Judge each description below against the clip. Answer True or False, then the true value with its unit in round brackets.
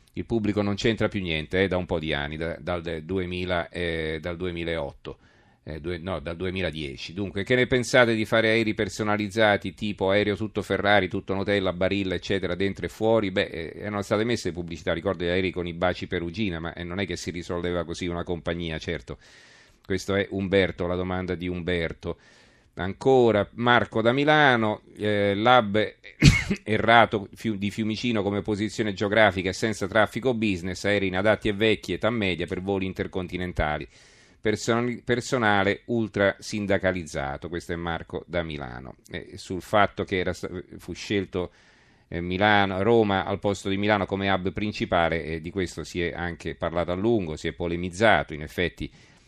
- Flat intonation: False (3.4 semitones)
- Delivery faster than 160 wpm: True (170 wpm)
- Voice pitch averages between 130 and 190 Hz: False (95 Hz)